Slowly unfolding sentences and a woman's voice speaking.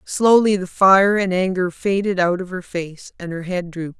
No: fast, 210 wpm; female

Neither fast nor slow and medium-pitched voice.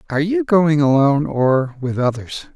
Yes: average, 165 wpm; medium, 150 Hz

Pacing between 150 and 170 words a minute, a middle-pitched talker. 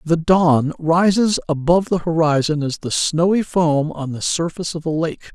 No: average, 180 wpm; medium, 160 Hz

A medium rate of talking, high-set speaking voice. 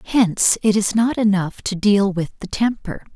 Yes: average, 190 wpm; high, 205 Hz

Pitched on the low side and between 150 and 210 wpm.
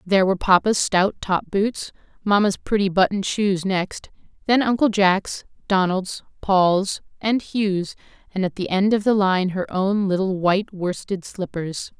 No: high, 195 Hz; average, 155 wpm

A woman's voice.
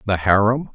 No: male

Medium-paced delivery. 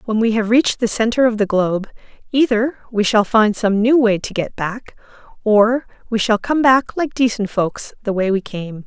No: fast, 210 wpm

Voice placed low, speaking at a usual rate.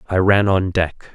No: very low, 95 Hz; fast, 210 wpm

